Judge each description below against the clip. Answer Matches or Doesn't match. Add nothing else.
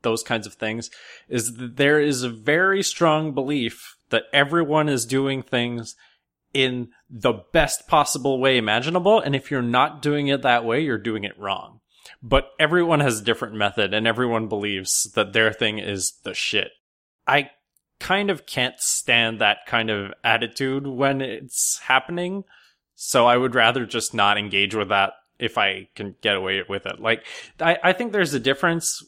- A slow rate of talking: Doesn't match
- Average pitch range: Matches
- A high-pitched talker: Doesn't match